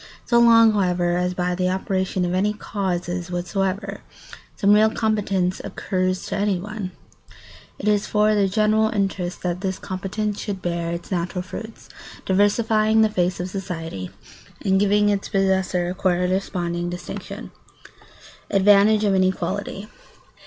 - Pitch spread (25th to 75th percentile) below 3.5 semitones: Yes, narrow, 2.5 semitones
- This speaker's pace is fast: No, average, 140 wpm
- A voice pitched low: No, high, 190 Hz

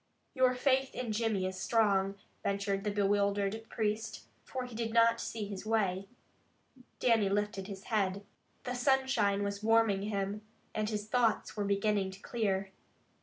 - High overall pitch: Yes, high, 210 Hz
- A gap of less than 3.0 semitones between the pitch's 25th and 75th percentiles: Yes, narrow, 2.4 semitones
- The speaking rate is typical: Yes, average, 150 wpm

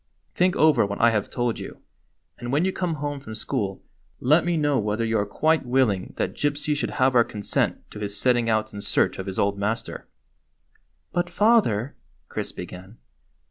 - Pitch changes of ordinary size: No, wide, 6.3 semitones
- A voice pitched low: Yes, low, 120 Hz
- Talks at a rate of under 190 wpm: No, average, 200 wpm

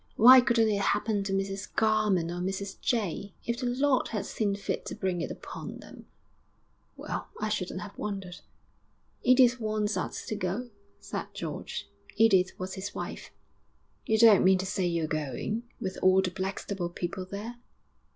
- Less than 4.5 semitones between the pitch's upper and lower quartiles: Yes, average, 2.8 semitones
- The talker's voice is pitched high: Yes, high, 200 Hz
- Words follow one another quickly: No, average, 165 wpm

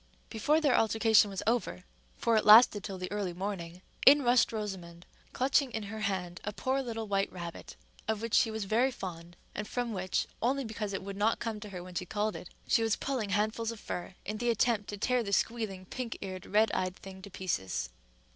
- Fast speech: Yes, fast, 215 wpm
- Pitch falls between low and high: No, high, 210 Hz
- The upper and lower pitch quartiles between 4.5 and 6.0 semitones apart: No, average, 3.4 semitones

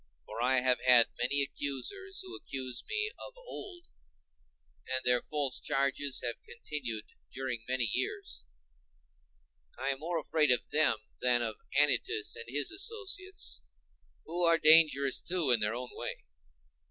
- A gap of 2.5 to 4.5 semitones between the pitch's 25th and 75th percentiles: No, average, 5.1 semitones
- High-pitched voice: No, medium, 140 Hz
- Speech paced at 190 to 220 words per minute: No, average, 145 wpm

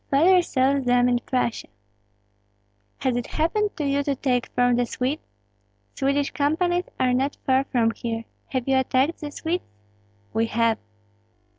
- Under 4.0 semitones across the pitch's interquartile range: Yes, average, 3.0 semitones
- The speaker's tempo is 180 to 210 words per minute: No, average, 150 wpm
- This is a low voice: No, very high, 265 Hz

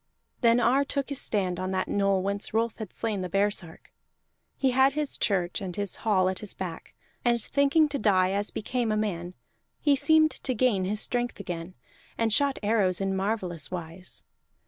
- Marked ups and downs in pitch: No, average, 4.7 semitones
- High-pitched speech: Yes, high, 205 Hz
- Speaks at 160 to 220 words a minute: Yes, average, 185 wpm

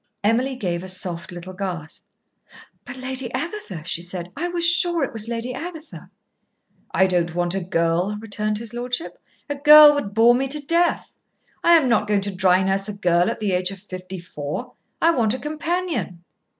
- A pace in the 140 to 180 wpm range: No, average, 190 wpm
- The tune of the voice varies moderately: No, wide, 7.2 semitones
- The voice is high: Yes, high, 215 Hz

